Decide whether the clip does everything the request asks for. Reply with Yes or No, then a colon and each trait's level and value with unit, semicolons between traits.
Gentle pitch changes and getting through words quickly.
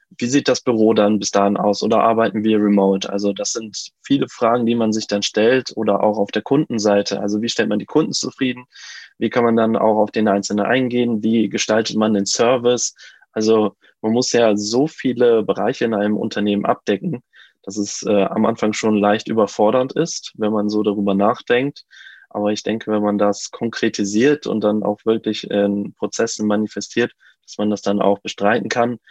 Yes: narrow, 2.1 semitones; fast, 195 wpm